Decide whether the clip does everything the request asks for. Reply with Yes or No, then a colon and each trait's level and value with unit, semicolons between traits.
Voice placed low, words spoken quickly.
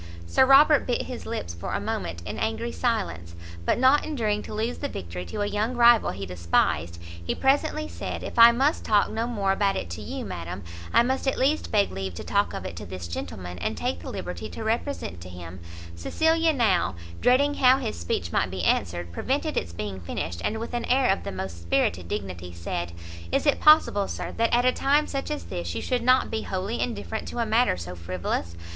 No: high, 190 Hz; fast, 220 wpm